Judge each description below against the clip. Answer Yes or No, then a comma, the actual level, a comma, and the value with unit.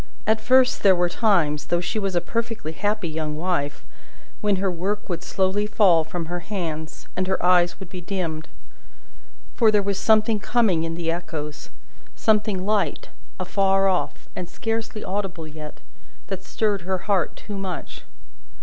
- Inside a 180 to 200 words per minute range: No, average, 160 wpm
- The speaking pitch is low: No, medium, 185 Hz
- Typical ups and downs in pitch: Yes, average, 3.3 semitones